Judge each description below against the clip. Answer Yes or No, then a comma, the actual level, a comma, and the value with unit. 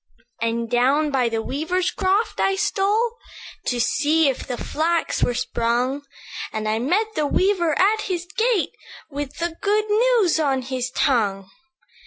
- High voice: Yes, very high, 295 Hz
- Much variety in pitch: Yes, wide, 7.4 semitones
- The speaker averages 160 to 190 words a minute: No, average, 150 wpm